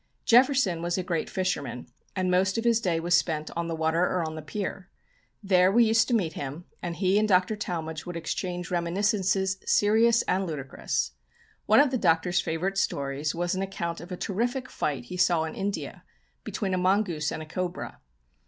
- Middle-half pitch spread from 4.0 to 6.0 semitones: No, average, 3.1 semitones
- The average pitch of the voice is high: No, medium, 180 Hz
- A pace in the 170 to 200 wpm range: Yes, average, 190 wpm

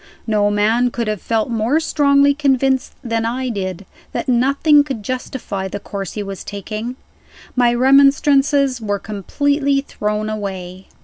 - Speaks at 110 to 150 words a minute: Yes, average, 140 wpm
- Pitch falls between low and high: No, high, 235 Hz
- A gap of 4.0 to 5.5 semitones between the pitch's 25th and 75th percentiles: Yes, average, 4.9 semitones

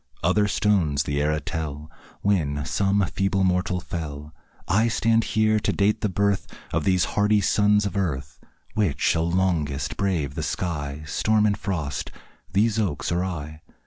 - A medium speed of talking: Yes, average, 155 wpm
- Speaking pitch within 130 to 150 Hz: No, very low, 90 Hz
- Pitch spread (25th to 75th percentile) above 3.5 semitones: Yes, average, 5.0 semitones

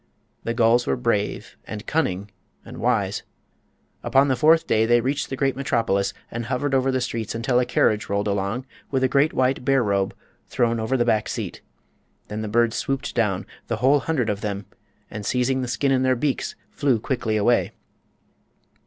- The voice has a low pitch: Yes, low, 120 Hz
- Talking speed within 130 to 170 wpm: No, average, 180 wpm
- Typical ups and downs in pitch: Yes, average, 3.6 semitones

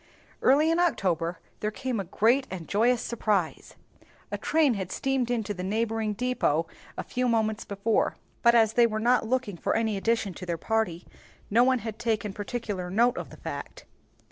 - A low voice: No, high, 225 Hz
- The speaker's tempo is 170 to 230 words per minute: Yes, average, 180 wpm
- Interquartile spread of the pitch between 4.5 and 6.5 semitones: No, average, 3.5 semitones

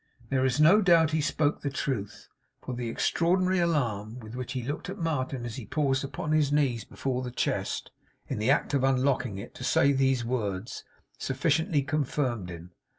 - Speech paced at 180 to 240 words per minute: Yes, average, 185 wpm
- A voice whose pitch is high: No, low, 135 Hz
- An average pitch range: Yes, average, 3.9 semitones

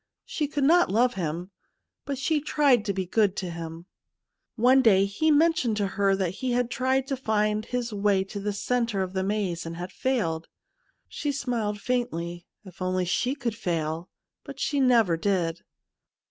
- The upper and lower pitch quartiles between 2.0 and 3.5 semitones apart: No, wide, 5.6 semitones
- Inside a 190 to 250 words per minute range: No, average, 180 wpm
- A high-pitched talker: Yes, high, 210 Hz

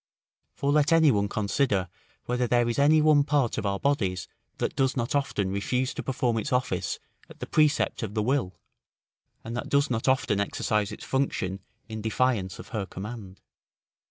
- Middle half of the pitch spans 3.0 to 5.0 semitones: No, wide, 5.4 semitones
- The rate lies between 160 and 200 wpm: Yes, average, 180 wpm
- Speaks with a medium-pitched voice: No, low, 120 Hz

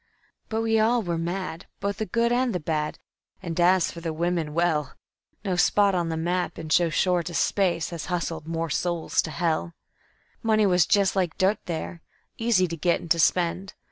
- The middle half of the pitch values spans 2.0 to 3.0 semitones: Yes, average, 2.7 semitones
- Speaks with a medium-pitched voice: Yes, medium, 175 Hz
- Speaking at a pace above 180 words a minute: Yes, average, 195 wpm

